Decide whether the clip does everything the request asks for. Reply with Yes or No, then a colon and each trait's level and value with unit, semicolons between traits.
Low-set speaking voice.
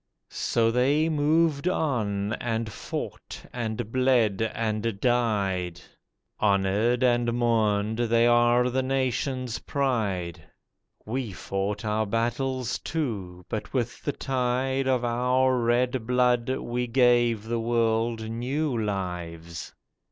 Yes: low, 120 Hz